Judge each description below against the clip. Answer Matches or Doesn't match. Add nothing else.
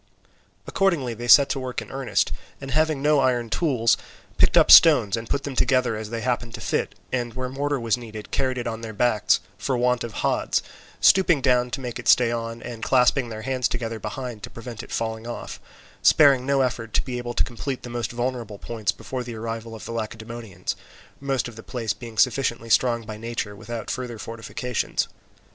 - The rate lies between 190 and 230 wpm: Matches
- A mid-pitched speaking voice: Doesn't match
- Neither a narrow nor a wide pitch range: Doesn't match